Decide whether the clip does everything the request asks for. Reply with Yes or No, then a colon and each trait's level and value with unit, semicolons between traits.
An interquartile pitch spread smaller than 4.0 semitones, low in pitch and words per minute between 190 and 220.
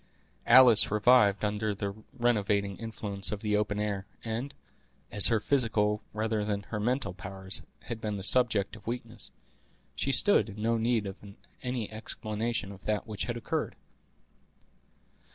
No: narrow, 2.4 semitones; low, 105 Hz; average, 150 wpm